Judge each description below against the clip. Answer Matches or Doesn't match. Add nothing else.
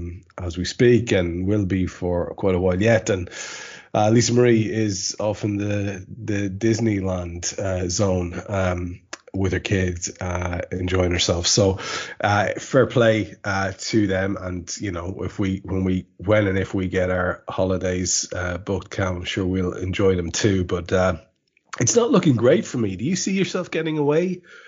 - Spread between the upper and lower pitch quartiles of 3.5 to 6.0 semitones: Doesn't match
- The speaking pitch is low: Matches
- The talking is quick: Doesn't match